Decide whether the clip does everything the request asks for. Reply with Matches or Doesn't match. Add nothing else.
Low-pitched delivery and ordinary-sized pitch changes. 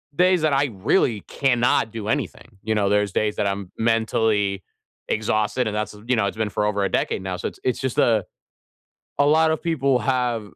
Matches